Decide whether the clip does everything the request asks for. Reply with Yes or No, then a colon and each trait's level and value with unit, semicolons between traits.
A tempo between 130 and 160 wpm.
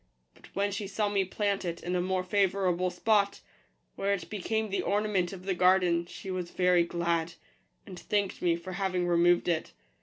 No: average, 185 wpm